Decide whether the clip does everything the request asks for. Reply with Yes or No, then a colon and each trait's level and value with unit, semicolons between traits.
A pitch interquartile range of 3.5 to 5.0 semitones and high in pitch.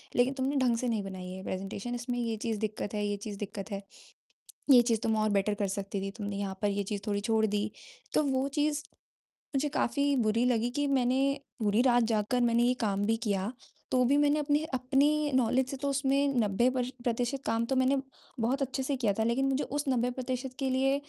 Yes: average, 4.0 semitones; high, 245 Hz